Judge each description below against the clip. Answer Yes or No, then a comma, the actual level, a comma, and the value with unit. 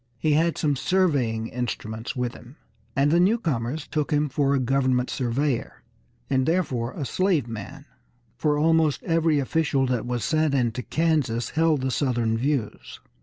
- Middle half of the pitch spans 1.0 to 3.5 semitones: No, average, 4.2 semitones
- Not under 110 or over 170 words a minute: Yes, average, 155 wpm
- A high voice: No, medium, 140 Hz